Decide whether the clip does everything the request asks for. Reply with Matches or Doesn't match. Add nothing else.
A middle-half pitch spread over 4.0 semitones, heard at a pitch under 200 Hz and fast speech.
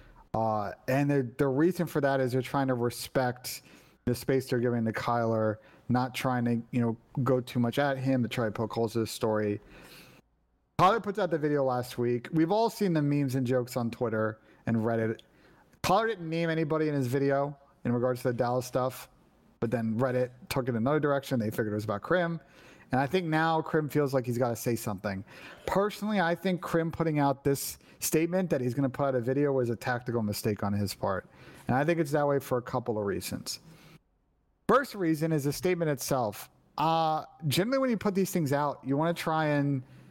Matches